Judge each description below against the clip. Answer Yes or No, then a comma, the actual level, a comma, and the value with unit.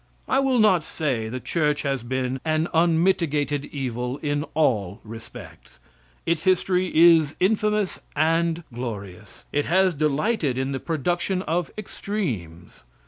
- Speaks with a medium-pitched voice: Yes, medium, 155 Hz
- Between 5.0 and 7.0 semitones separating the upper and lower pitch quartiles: Yes, average, 5.3 semitones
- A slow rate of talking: Yes, slow, 130 wpm